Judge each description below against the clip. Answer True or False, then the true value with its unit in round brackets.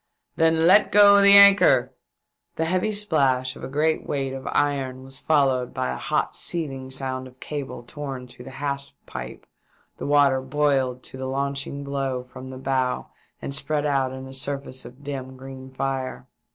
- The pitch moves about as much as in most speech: False (1.9 semitones)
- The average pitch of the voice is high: False (135 Hz)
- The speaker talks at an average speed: True (180 wpm)